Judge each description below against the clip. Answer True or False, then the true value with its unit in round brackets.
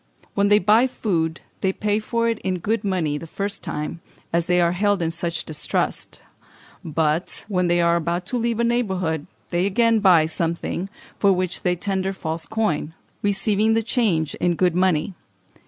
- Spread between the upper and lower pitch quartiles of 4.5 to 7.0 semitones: False (3.7 semitones)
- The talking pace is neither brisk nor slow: True (175 wpm)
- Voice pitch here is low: False (185 Hz)